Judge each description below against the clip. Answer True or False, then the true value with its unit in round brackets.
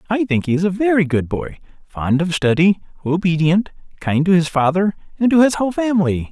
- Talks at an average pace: True (190 wpm)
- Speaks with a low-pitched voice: False (180 Hz)